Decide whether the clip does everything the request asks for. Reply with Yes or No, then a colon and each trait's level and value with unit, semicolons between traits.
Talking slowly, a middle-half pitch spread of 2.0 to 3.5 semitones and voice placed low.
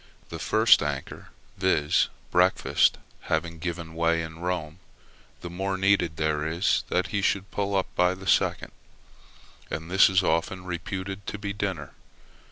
No: average, 150 wpm; average, 2.9 semitones; very low, 90 Hz